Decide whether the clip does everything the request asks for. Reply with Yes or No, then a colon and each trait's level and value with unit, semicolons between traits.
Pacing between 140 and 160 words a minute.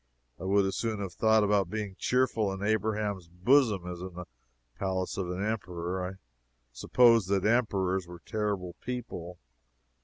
Yes: average, 155 wpm